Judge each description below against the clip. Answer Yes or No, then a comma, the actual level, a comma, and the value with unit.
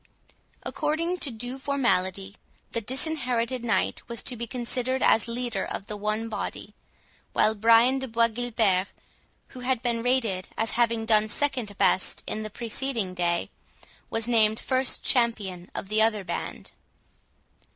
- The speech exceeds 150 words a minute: No, average, 145 wpm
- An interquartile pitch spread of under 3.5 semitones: Yes, average, 2.8 semitones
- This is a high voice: Yes, high, 230 Hz